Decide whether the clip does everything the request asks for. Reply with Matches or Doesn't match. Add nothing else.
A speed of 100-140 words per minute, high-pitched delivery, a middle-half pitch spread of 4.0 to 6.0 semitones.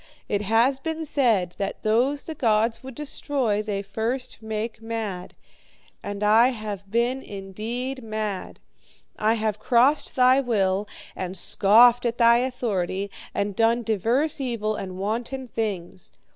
Doesn't match